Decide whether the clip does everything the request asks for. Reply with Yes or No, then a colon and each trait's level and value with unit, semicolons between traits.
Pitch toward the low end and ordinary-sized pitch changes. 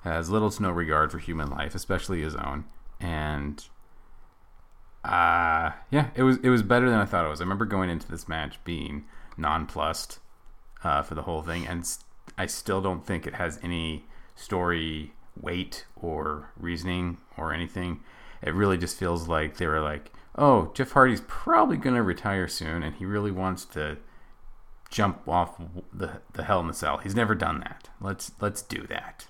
Yes: very low, 85 Hz; average, 3.1 semitones